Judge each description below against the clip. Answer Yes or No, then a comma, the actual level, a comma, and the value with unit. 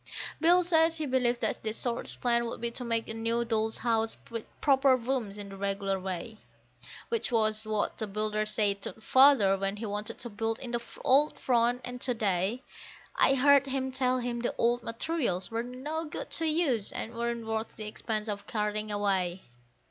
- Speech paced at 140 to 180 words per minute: No, average, 195 wpm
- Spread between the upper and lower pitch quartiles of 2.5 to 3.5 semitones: Yes, average, 3.2 semitones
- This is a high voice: Yes, high, 230 Hz